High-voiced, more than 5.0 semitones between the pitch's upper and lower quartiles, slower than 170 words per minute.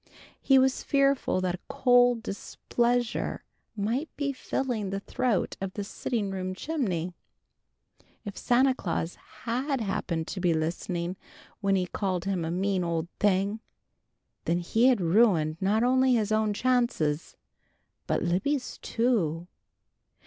Yes: high, 205 Hz; wide, 5.4 semitones; slow, 135 wpm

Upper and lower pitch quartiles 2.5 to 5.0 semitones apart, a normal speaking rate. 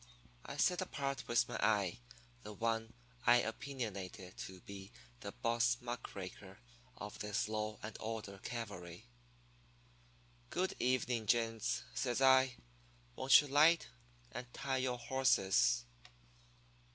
No: average, 4.0 semitones; slow, 120 wpm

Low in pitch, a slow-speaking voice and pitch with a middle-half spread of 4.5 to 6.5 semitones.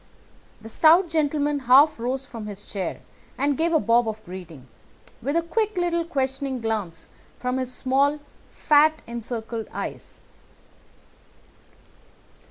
No: very high, 265 Hz; slow, 125 wpm; wide, 5.4 semitones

